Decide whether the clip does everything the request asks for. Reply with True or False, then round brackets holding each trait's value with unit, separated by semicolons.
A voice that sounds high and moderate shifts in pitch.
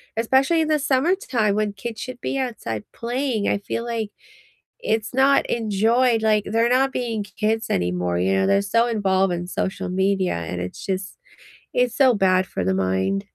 True (215 Hz; 5.0 semitones)